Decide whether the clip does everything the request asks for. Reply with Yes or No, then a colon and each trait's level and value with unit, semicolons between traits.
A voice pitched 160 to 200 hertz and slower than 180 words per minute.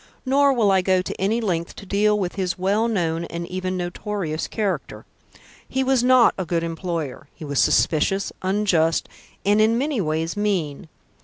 Yes: high, 190 Hz; average, 170 wpm